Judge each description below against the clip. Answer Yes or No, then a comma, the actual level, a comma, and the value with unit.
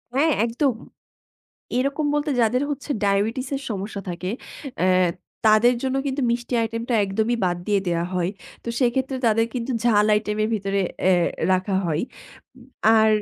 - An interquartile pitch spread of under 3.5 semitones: No, average, 4.5 semitones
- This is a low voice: No, high, 225 Hz